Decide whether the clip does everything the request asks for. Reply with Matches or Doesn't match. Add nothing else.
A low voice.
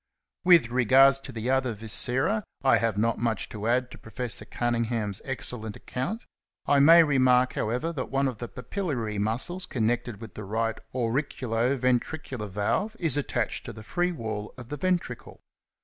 Matches